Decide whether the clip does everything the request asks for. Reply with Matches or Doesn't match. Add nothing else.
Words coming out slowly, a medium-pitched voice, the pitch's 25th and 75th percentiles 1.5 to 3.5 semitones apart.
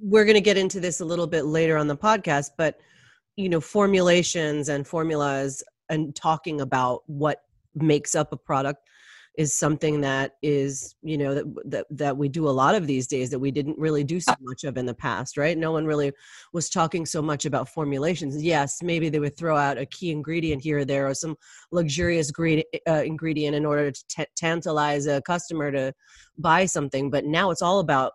Doesn't match